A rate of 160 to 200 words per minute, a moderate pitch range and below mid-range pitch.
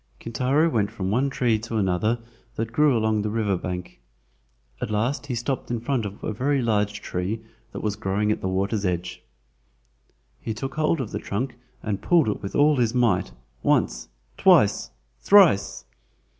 Yes: average, 170 wpm; average, 4.1 semitones; low, 110 Hz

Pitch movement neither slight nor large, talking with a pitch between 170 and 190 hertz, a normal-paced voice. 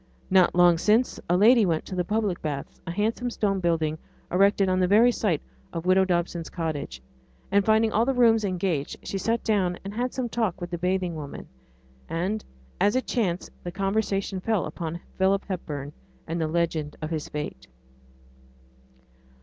Yes: average, 4.0 semitones; medium, 185 Hz; average, 175 wpm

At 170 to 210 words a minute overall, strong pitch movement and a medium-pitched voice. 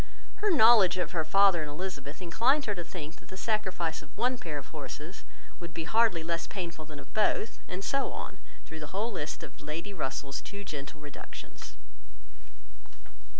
No: average, 180 wpm; average, 4.8 semitones; medium, 170 Hz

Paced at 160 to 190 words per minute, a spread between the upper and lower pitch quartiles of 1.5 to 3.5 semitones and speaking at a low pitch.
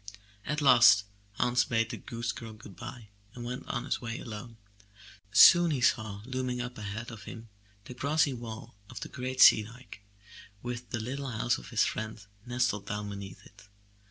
Yes: average, 180 wpm; average, 2.8 semitones; low, 120 Hz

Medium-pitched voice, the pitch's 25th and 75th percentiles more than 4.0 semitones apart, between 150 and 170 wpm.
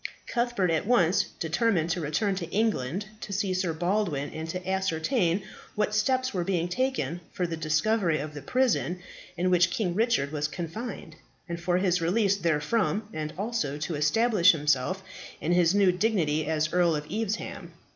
Yes: medium, 180 Hz; average, 4.6 semitones; average, 165 wpm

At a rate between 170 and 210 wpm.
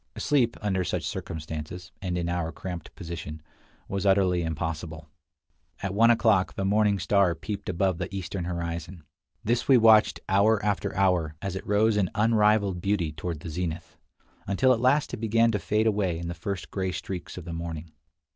Yes: average, 175 wpm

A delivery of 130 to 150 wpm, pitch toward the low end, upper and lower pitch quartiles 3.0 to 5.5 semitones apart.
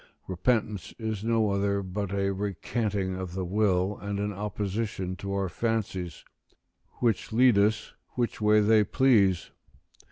No: slow, 135 wpm; low, 100 Hz; narrow, 2.4 semitones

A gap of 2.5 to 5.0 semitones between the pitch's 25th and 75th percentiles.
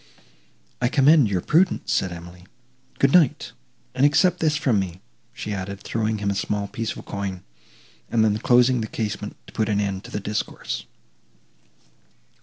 Yes: average, 4.3 semitones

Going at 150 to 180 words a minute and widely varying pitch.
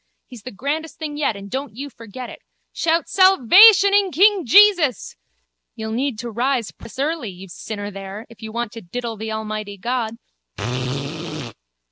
Yes: average, 160 wpm; wide, 6.3 semitones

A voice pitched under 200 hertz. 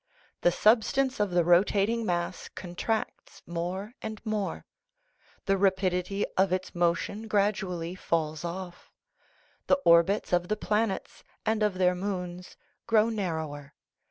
Yes: high, 190 Hz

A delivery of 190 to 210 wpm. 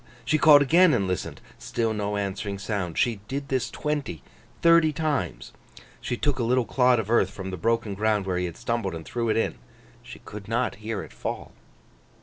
Yes: average, 195 wpm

